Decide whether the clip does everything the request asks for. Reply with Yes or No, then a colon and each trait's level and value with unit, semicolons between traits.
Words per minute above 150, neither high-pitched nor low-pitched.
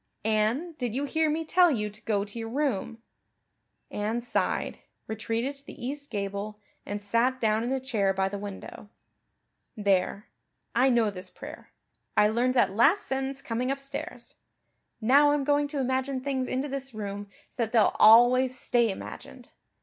No: average, 165 wpm; high, 240 Hz